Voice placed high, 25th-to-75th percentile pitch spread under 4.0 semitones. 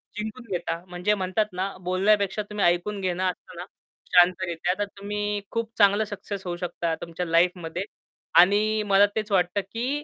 Yes: high, 195 Hz; average, 2.8 semitones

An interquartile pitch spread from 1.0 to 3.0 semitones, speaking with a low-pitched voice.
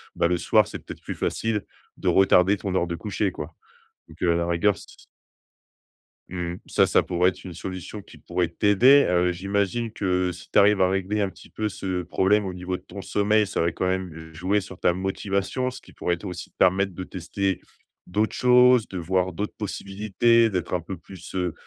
Yes: narrow, 2.5 semitones; very low, 95 Hz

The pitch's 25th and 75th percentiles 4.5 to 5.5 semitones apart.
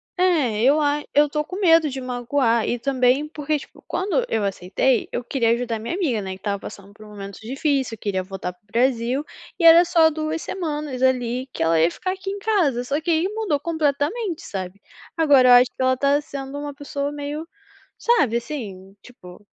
Yes: average, 5.2 semitones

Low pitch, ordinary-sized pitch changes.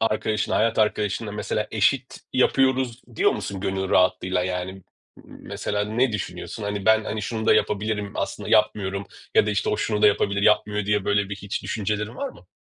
No: low, 105 Hz; narrow, 1.7 semitones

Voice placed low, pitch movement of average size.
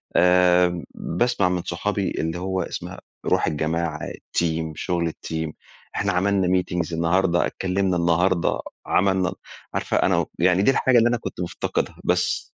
No: very low, 90 Hz; narrow, 2.0 semitones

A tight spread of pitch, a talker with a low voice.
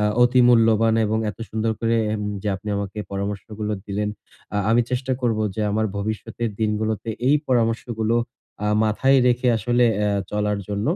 Yes: narrow, 2.0 semitones; low, 110 Hz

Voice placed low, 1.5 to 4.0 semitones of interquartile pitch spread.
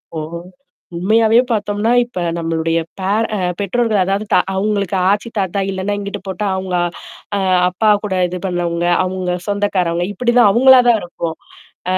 No: high, 195 Hz; average, 3.0 semitones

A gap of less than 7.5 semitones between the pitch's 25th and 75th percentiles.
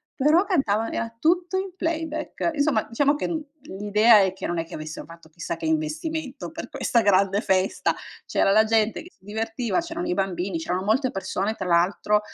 No: wide, 8.2 semitones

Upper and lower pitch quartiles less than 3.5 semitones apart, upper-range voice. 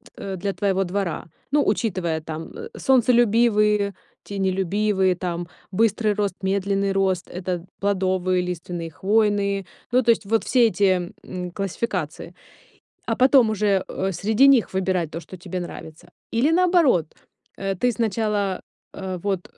Yes: average, 3.0 semitones; high, 195 Hz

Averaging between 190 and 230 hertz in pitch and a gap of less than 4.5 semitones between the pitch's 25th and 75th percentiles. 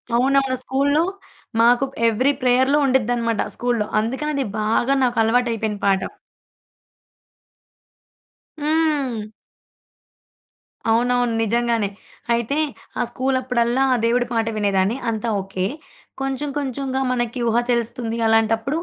No: high, 240 Hz; average, 2.8 semitones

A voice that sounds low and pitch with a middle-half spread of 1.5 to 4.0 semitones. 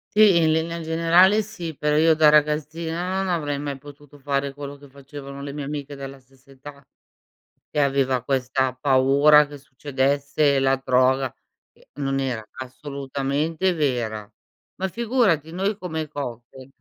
No: medium, 145 Hz; average, 2.8 semitones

